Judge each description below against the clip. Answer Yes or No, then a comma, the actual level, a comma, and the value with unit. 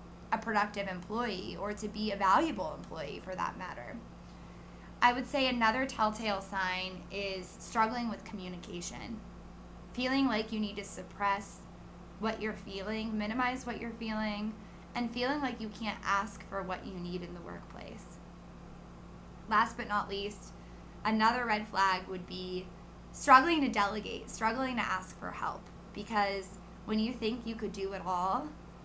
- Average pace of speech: Yes, average, 155 wpm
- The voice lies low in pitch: No, high, 210 Hz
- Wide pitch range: No, average, 2.7 semitones